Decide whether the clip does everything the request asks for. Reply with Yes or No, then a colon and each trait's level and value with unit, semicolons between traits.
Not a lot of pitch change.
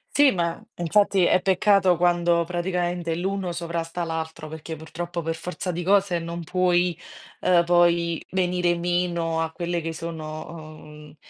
Yes: narrow, 1.5 semitones